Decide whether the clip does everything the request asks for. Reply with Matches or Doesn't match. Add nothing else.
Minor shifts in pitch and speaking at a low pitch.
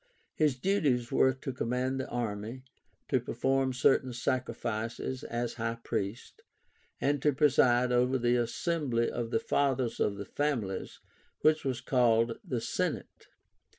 Matches